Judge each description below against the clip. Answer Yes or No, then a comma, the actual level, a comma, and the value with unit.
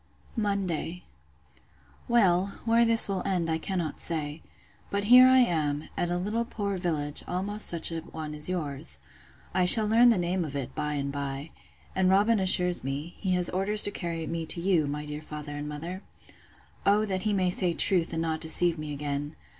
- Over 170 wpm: Yes, average, 190 wpm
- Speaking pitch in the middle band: Yes, medium, 175 Hz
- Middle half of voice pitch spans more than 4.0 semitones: Yes, average, 4.5 semitones